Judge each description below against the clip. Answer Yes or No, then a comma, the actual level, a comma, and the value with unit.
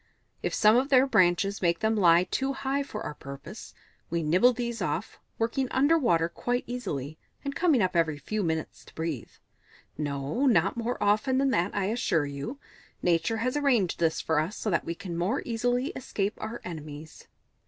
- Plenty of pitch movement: Yes, wide, 6.8 semitones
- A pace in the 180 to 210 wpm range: Yes, average, 185 wpm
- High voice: Yes, high, 205 Hz